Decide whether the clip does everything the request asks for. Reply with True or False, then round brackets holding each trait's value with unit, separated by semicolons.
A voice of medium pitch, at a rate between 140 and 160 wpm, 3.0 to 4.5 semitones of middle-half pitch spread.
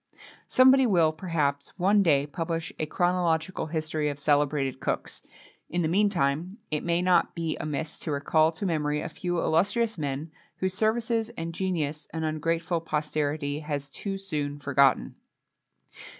True (160 Hz; 145 wpm; 3.3 semitones)